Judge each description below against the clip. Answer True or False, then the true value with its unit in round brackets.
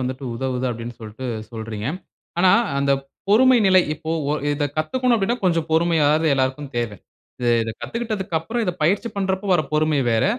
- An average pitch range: False (6.6 semitones)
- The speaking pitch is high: False (155 Hz)